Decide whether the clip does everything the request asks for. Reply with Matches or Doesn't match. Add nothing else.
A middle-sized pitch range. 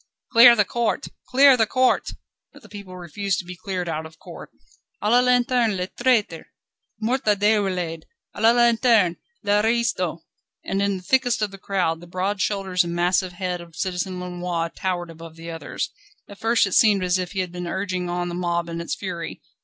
Matches